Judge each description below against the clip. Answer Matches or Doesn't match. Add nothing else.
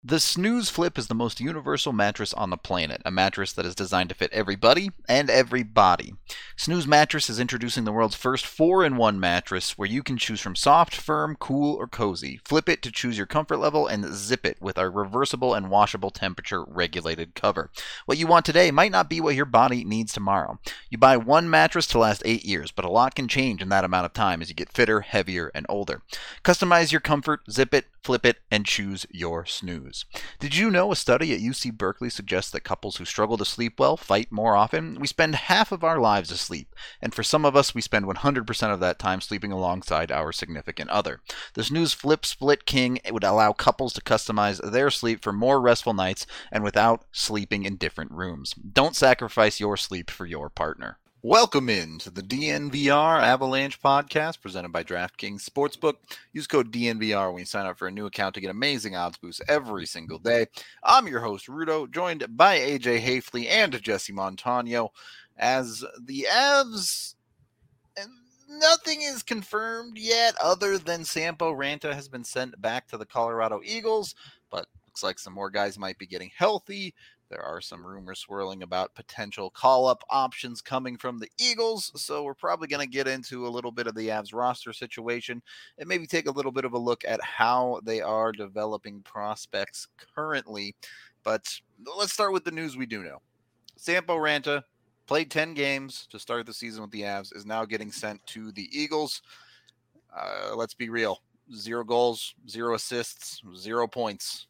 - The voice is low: Matches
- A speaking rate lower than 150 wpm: Doesn't match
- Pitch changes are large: Matches